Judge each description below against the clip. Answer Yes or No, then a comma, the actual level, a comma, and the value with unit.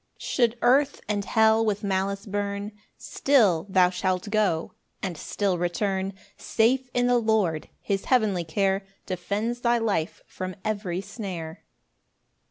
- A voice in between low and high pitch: No, high, 200 Hz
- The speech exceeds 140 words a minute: No, slow, 135 wpm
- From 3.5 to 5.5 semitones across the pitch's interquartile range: No, average, 3.1 semitones